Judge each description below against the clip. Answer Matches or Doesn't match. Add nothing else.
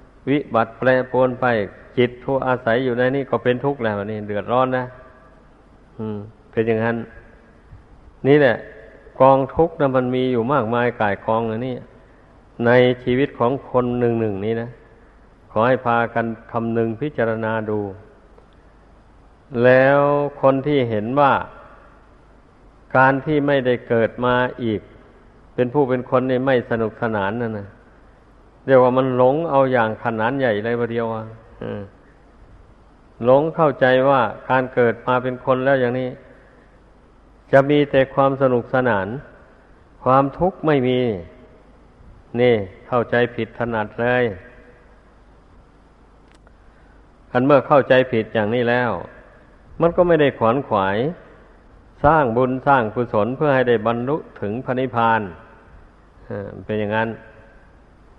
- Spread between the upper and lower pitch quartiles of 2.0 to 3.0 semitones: Matches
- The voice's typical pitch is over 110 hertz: Matches